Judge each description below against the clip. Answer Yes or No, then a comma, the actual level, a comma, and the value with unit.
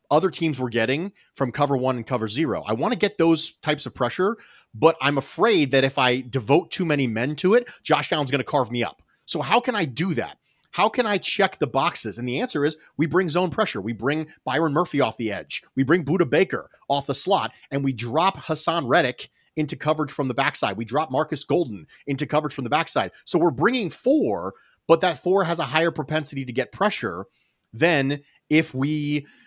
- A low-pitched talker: No, medium, 150 Hz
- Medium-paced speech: No, fast, 220 wpm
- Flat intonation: No, average, 3.7 semitones